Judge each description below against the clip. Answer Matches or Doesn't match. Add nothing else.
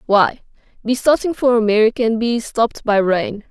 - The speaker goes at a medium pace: Matches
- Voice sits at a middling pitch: Doesn't match